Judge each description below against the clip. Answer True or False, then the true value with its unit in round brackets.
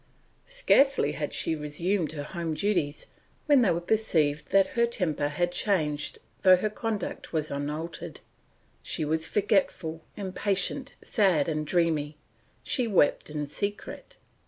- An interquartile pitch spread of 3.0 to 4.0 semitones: False (5.0 semitones)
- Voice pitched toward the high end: False (170 Hz)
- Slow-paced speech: True (130 wpm)